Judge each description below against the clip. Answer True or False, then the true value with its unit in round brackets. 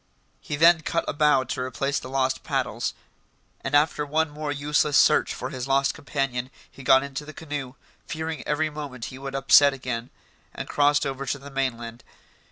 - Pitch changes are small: True (2.1 semitones)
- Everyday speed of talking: True (180 wpm)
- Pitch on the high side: False (140 Hz)